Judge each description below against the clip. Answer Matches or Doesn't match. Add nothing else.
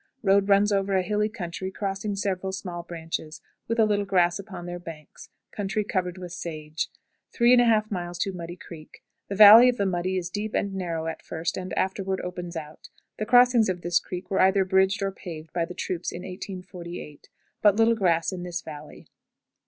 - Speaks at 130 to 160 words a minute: Doesn't match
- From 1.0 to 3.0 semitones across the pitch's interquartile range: Matches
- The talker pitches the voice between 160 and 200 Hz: Matches